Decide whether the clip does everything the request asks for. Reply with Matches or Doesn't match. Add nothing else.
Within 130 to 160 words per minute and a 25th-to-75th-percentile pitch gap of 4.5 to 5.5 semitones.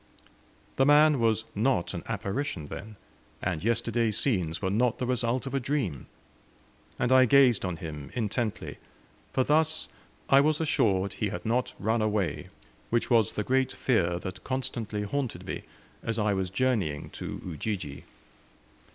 Matches